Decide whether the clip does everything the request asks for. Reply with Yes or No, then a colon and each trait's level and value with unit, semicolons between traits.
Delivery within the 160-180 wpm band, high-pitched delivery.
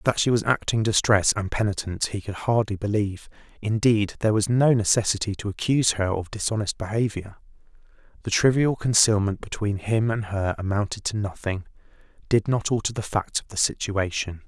No: average, 165 wpm; low, 105 Hz